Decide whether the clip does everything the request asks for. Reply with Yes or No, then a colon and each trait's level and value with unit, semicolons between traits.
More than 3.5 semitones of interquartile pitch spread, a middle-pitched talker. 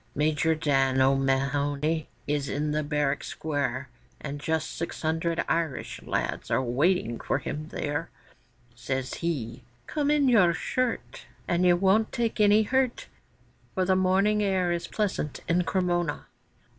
Yes: average, 4.8 semitones; medium, 160 Hz